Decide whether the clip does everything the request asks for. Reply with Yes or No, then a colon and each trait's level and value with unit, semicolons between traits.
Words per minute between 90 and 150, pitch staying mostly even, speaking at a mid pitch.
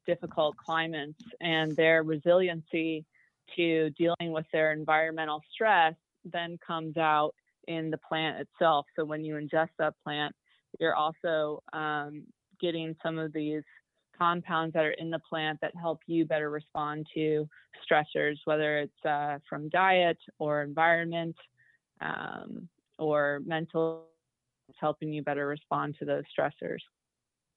Yes: slow, 135 wpm; narrow, 1.5 semitones; medium, 160 Hz